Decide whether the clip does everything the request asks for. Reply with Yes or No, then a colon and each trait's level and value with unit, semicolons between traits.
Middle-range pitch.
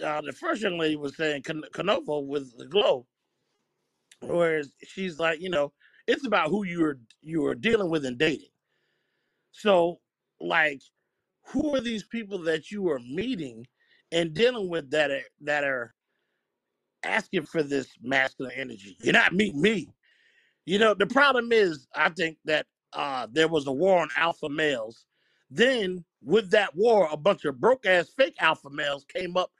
Yes: medium, 170 Hz